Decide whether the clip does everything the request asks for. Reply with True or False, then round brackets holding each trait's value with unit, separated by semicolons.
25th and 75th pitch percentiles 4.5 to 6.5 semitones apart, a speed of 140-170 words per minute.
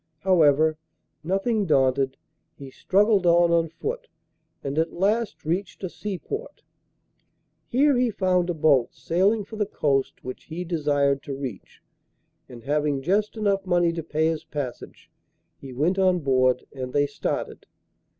True (5.6 semitones; 145 wpm)